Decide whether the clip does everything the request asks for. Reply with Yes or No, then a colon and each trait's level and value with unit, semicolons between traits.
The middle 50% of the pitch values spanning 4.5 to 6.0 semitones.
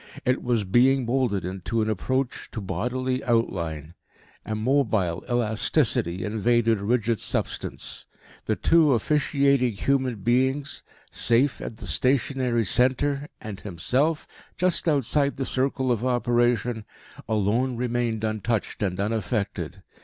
No: average, 3.5 semitones